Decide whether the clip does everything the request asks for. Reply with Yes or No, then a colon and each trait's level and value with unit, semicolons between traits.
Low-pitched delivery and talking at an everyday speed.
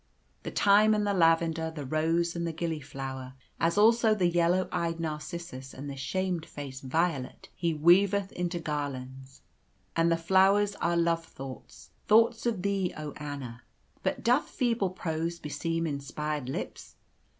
No: medium, 165 Hz; average, 145 wpm